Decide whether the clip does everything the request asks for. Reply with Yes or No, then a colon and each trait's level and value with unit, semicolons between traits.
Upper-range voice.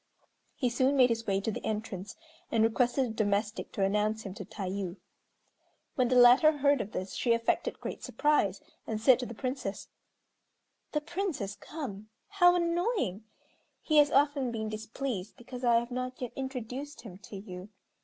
Yes: high, 235 Hz